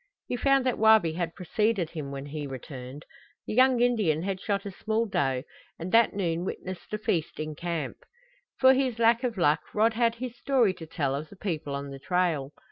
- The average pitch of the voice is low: No, medium, 185 Hz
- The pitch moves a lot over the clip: Yes, wide, 6.7 semitones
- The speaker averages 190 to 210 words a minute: Yes, fast, 205 wpm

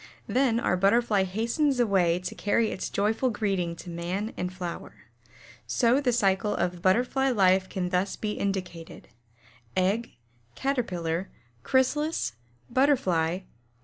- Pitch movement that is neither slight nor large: Yes, average, 4.8 semitones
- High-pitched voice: Yes, high, 200 Hz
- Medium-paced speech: No, slow, 125 wpm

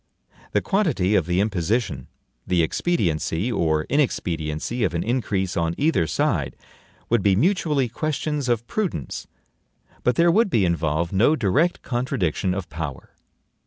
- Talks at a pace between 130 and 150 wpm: Yes, slow, 135 wpm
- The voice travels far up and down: Yes, wide, 8.5 semitones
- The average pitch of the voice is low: Yes, low, 100 Hz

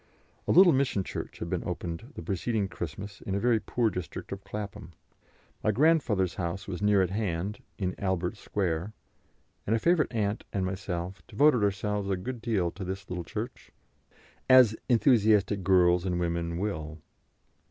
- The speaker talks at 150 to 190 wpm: Yes, average, 165 wpm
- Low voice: Yes, low, 100 Hz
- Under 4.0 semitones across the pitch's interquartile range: Yes, average, 3.3 semitones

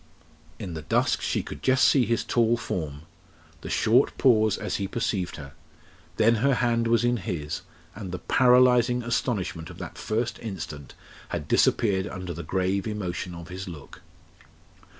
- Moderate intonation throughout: Yes, average, 5.0 semitones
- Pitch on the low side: Yes, low, 105 Hz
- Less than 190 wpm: Yes, average, 160 wpm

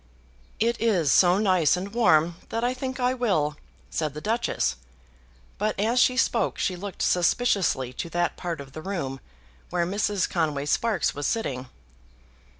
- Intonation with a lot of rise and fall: Yes, wide, 6.5 semitones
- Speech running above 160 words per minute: No, average, 155 wpm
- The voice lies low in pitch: No, medium, 185 Hz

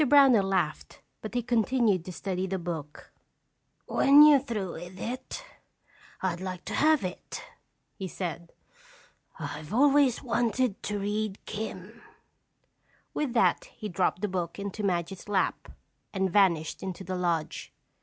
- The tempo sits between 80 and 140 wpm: Yes, slow, 135 wpm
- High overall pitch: Yes, high, 195 Hz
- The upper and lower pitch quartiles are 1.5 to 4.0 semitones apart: No, average, 4.7 semitones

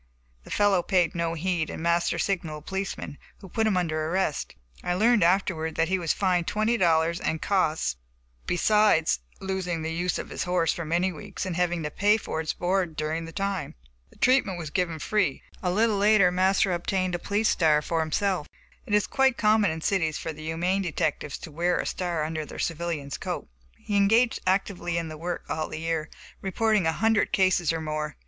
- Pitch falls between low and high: Yes, medium, 175 Hz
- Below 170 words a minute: No, average, 200 wpm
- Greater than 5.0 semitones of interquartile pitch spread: No, average, 3.4 semitones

